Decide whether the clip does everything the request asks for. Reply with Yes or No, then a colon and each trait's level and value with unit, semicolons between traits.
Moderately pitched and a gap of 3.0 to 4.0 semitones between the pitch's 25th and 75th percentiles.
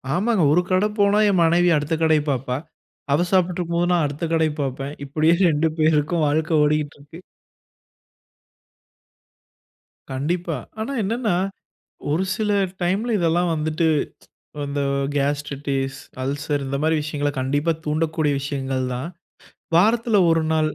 Yes: medium, 155 Hz; average, 3.3 semitones